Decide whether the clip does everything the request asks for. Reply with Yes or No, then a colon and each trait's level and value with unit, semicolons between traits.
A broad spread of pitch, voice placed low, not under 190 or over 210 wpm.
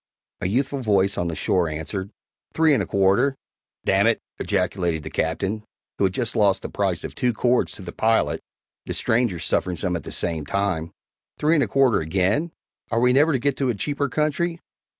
Yes: wide, 6.4 semitones; low, 105 Hz; average, 200 wpm